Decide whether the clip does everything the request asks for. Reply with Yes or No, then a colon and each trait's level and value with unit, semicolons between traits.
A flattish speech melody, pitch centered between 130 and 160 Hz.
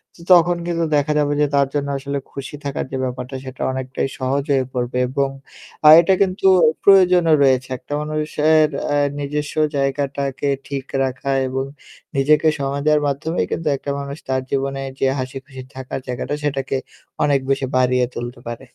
Yes: narrow, 2.1 semitones; medium, 140 Hz